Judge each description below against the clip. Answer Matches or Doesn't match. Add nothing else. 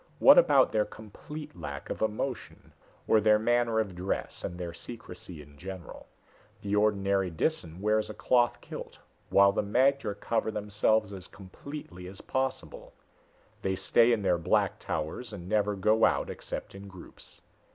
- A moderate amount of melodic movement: Matches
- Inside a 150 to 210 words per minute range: Matches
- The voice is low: Matches